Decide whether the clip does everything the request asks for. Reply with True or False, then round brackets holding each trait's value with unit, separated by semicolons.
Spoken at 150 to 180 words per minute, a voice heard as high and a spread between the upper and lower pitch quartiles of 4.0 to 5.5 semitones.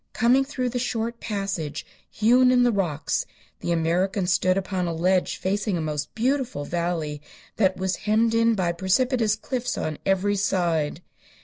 True (155 wpm; 195 Hz; 5.0 semitones)